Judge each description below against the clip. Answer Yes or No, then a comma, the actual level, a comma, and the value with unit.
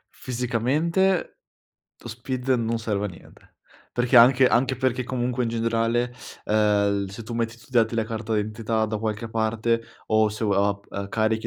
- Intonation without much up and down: Yes, narrow, 2.0 semitones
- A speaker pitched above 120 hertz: No, low, 115 Hz